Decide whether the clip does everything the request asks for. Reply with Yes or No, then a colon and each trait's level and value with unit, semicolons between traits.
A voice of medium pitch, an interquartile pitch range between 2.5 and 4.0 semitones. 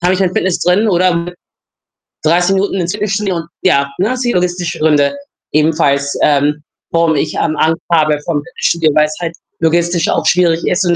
Yes: medium, 170 Hz; average, 2.8 semitones